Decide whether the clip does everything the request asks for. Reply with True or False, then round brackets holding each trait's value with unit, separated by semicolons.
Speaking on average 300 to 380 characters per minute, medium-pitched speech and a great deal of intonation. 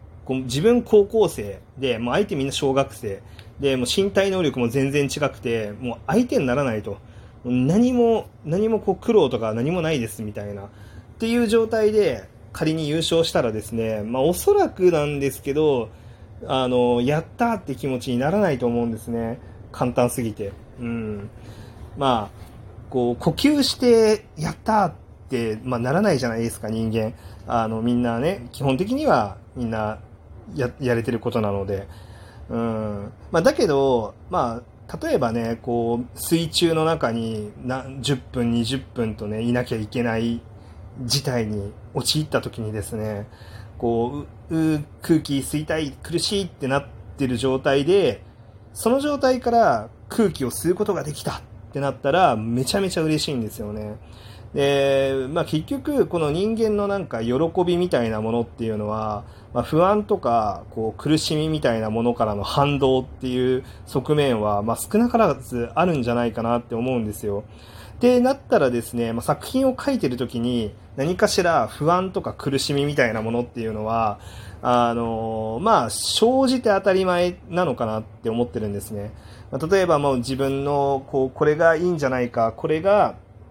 False (325 characters per minute; 125 Hz; 6.1 semitones)